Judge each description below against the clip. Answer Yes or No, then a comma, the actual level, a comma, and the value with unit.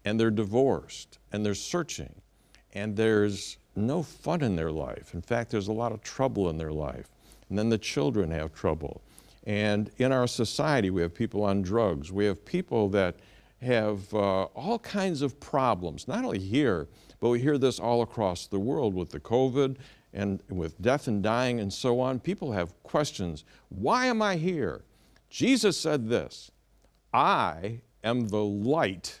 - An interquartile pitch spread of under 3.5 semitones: No, average, 4.6 semitones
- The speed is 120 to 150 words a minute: No, average, 175 wpm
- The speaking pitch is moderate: No, low, 110 Hz